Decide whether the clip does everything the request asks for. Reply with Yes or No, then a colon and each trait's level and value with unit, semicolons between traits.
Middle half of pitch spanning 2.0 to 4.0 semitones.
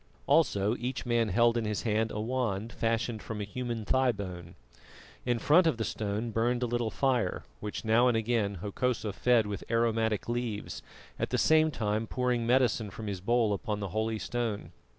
Yes: narrow, 2.4 semitones